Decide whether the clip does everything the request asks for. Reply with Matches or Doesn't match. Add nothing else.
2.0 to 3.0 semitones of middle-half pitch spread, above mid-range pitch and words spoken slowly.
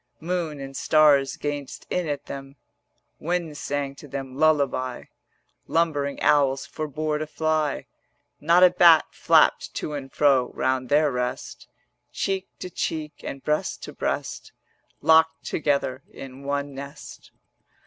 Doesn't match